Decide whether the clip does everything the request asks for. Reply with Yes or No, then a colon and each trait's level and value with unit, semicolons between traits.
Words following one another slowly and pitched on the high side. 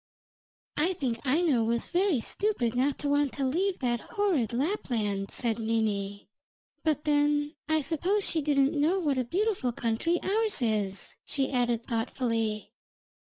No: average, 145 wpm; very high, 275 Hz